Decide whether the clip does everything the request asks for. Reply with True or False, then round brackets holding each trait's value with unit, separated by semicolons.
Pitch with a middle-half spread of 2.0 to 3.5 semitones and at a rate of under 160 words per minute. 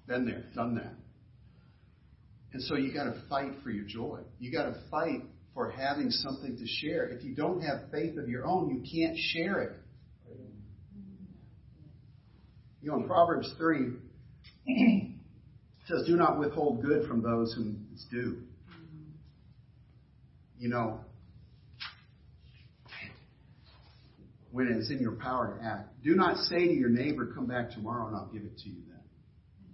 False (4.1 semitones; 150 wpm)